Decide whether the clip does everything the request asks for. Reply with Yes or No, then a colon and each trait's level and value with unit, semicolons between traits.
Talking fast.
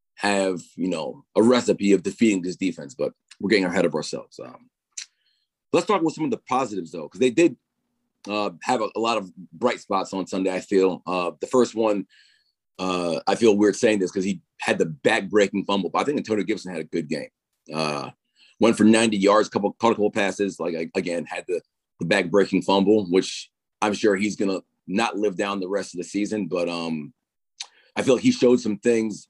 Yes: fast, 215 wpm